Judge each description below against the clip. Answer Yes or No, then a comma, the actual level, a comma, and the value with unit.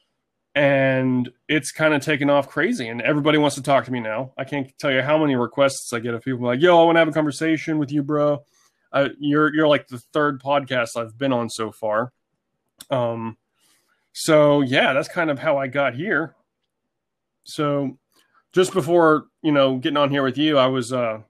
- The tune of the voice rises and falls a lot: No, average, 3.1 semitones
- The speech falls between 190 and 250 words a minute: Yes, fast, 205 wpm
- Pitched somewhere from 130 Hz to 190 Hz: Yes, medium, 140 Hz